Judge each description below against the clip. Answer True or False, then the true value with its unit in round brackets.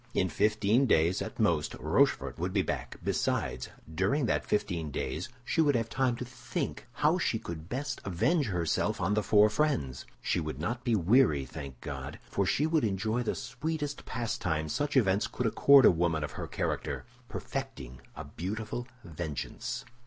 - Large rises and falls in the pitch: True (7.1 semitones)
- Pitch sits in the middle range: False (105 Hz)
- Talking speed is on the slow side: False (165 wpm)